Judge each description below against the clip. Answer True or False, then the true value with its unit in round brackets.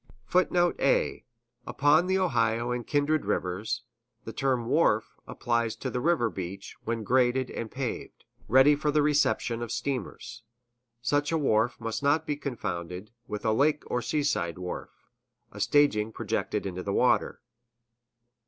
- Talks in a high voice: False (125 Hz)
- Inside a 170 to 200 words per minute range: False (145 wpm)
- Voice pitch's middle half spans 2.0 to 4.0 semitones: False (4.7 semitones)